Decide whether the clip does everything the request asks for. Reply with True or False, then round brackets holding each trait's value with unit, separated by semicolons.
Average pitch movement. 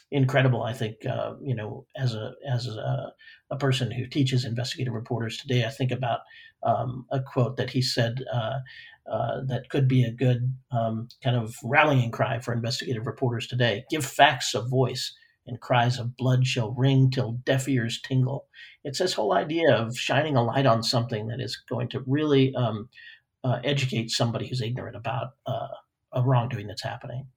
False (2.1 semitones)